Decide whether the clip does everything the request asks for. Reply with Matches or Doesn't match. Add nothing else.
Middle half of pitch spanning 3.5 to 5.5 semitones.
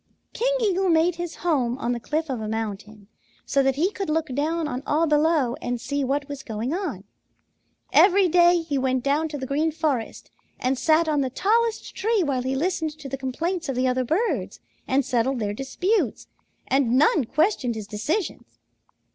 Matches